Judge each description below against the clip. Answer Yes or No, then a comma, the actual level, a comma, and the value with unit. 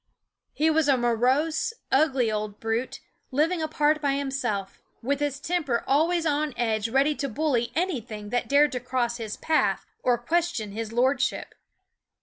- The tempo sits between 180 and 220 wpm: No, average, 155 wpm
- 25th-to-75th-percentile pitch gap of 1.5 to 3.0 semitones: No, average, 4.4 semitones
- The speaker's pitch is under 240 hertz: No, very high, 270 Hz